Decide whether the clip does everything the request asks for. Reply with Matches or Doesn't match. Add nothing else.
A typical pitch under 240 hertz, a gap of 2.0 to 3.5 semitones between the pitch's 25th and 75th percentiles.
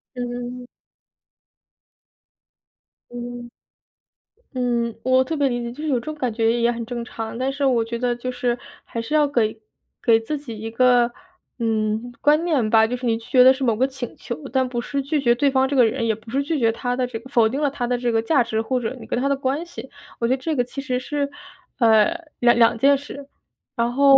Doesn't match